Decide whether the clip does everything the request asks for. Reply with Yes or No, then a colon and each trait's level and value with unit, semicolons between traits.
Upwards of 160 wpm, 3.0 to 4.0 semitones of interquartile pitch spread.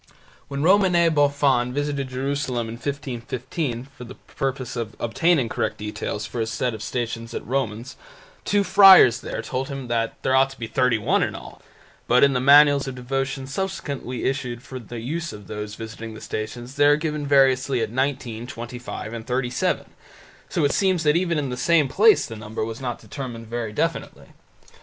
Yes: average, 190 wpm; average, 3.4 semitones